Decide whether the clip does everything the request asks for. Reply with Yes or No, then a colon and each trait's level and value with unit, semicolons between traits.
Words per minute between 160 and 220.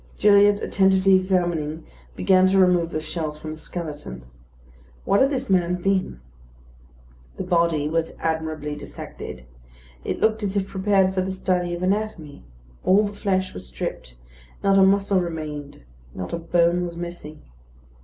No: average, 150 wpm